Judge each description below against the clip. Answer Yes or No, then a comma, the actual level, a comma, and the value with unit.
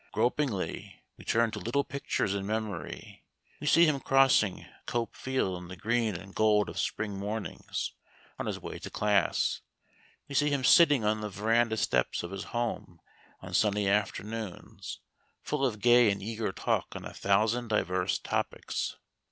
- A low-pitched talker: Yes, low, 110 Hz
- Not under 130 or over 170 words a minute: Yes, average, 160 wpm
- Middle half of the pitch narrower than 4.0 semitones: Yes, average, 3.3 semitones